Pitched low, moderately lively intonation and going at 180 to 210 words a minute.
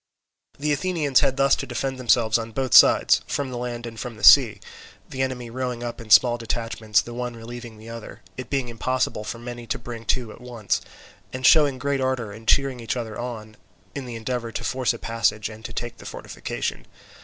No: low, 120 Hz; narrow, 2.2 semitones; average, 200 wpm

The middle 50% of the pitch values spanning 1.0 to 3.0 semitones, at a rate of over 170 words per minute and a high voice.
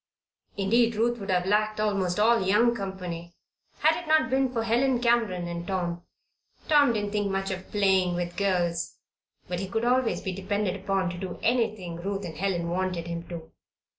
No: average, 4.2 semitones; average, 180 wpm; high, 195 Hz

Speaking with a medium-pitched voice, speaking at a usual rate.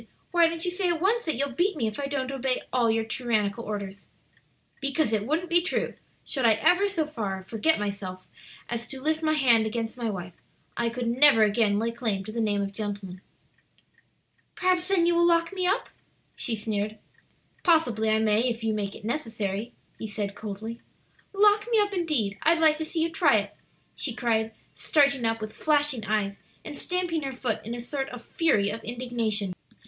No: high, 235 Hz; average, 195 wpm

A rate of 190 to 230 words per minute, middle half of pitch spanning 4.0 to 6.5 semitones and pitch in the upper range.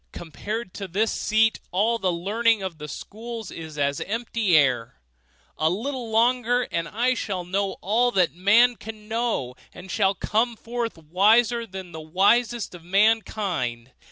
No: average, 155 wpm; average, 4.8 semitones; high, 205 Hz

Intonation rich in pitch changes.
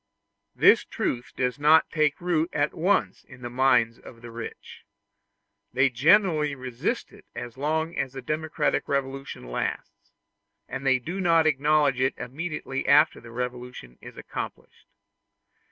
No: average, 3.8 semitones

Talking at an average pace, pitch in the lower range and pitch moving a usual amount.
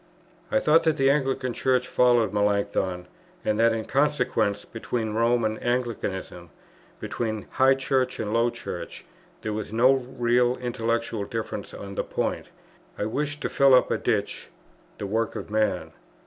Yes: average, 155 wpm; low, 115 Hz; average, 3.2 semitones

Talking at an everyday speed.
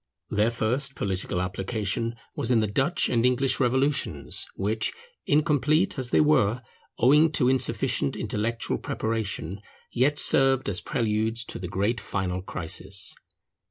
No: slow, 130 wpm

